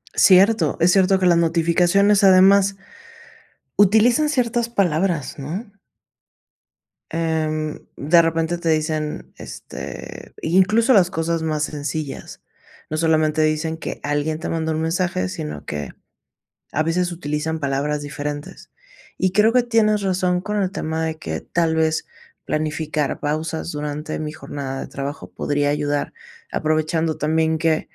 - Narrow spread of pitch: No, average, 3.2 semitones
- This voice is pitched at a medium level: Yes, medium, 160 Hz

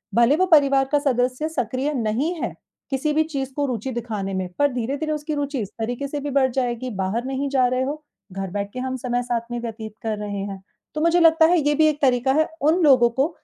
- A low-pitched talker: No, very high, 265 Hz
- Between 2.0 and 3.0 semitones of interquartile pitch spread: No, average, 3.7 semitones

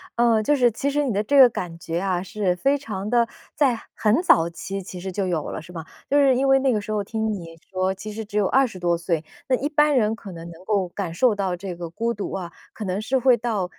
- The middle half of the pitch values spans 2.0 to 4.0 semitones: No, average, 5.2 semitones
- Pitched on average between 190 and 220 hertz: Yes, high, 205 Hz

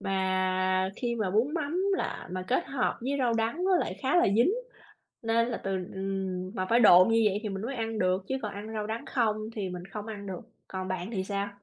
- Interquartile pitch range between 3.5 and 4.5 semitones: Yes, average, 3.9 semitones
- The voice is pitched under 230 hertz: Yes, high, 210 Hz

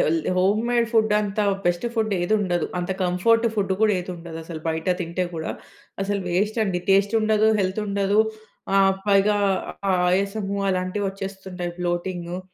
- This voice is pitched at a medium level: No, high, 195 Hz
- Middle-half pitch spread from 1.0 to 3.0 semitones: Yes, average, 2.7 semitones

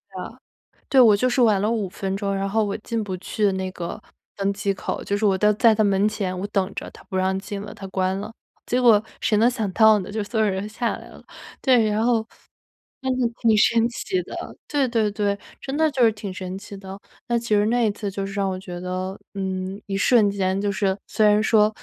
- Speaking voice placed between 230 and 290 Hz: No, high, 205 Hz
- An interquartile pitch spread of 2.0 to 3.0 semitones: Yes, narrow, 2.4 semitones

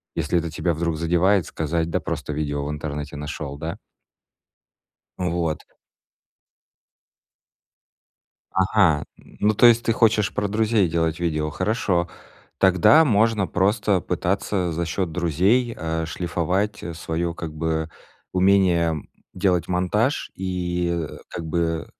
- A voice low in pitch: Yes, very low, 85 Hz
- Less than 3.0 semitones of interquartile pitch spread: No, average, 3.3 semitones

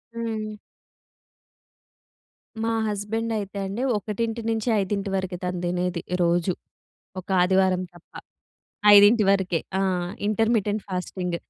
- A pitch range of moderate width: Yes, average, 3.2 semitones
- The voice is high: Yes, high, 200 Hz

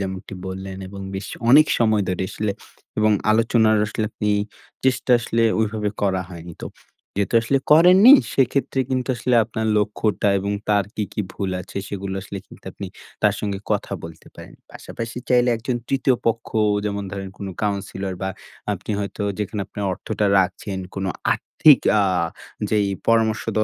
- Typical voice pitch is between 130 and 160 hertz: No, low, 105 Hz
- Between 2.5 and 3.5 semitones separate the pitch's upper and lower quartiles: Yes, average, 2.8 semitones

